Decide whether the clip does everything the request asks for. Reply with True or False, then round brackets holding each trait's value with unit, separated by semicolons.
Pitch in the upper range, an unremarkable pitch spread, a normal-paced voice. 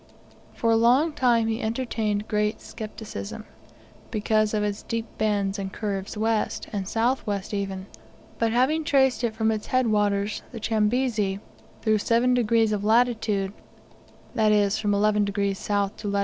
False (215 Hz; 2.1 semitones; 160 wpm)